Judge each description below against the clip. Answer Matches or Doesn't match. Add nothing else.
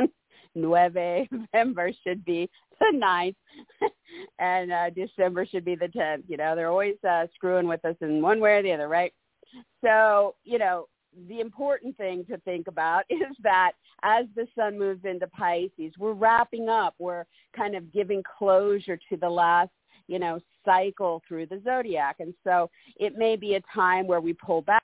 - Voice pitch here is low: Doesn't match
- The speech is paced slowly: Doesn't match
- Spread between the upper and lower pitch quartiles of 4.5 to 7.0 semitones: Doesn't match